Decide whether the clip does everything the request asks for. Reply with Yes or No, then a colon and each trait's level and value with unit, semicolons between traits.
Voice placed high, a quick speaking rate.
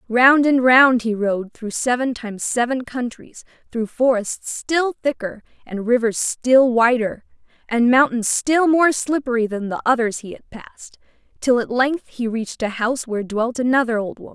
No: high, 240 Hz; average, 170 wpm